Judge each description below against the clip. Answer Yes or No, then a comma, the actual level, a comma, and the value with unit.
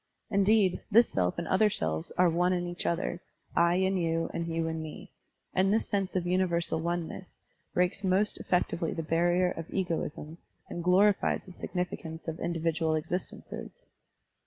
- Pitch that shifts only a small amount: Yes, narrow, 2.2 semitones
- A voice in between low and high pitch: Yes, medium, 175 Hz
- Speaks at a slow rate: No, average, 160 wpm